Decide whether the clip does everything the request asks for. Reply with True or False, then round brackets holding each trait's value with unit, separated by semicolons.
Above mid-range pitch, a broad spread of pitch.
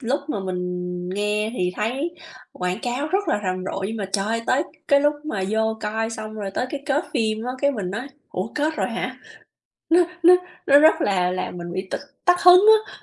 True (220 Hz; 6.6 semitones)